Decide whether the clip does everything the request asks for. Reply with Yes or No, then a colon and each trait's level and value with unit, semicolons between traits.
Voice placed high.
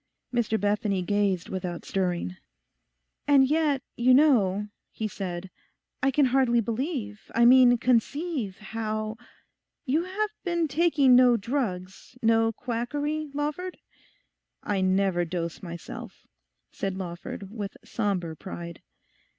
Yes: high, 225 Hz